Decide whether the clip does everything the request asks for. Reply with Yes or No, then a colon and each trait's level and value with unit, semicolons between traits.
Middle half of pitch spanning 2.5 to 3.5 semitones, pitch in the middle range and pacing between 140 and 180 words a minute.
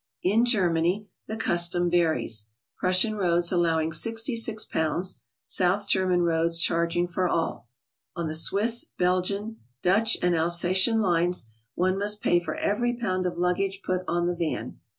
Yes: average, 2.9 semitones; medium, 180 Hz; average, 145 wpm